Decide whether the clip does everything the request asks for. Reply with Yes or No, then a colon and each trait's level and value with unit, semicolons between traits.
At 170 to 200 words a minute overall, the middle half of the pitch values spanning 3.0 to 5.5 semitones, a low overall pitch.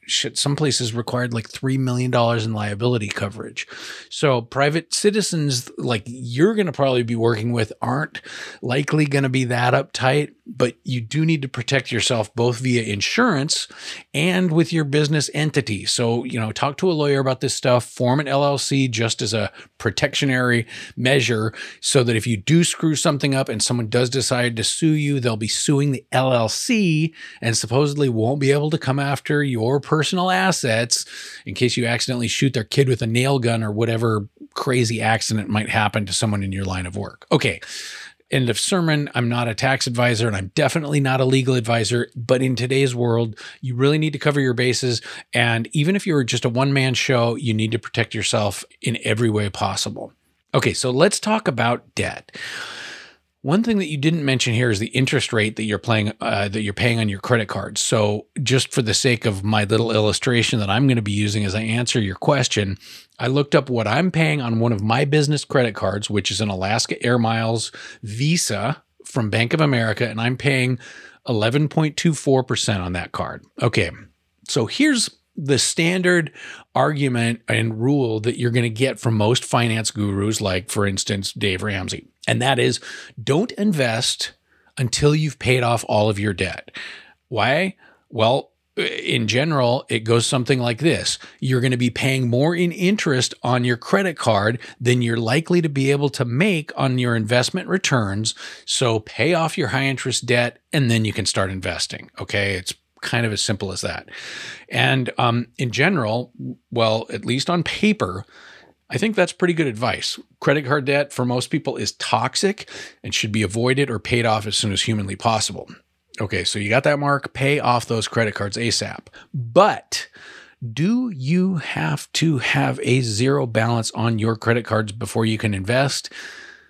Yes: average, 185 wpm; average, 4.2 semitones; low, 125 Hz